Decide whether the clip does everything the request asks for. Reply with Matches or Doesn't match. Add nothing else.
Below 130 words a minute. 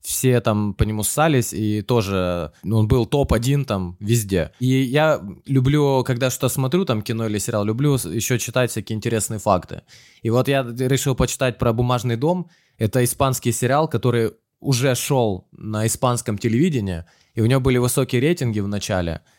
Doesn't match